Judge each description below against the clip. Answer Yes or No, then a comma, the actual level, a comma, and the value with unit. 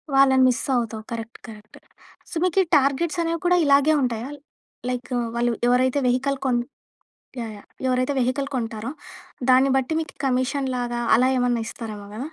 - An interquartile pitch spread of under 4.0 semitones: Yes, narrow, 2.6 semitones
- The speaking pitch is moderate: No, very high, 255 Hz